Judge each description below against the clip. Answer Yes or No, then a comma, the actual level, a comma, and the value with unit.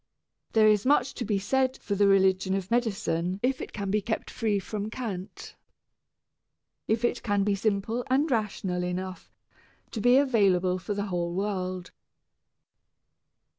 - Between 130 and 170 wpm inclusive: Yes, average, 150 wpm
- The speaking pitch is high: Yes, high, 205 Hz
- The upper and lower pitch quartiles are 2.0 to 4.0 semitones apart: Yes, average, 3.4 semitones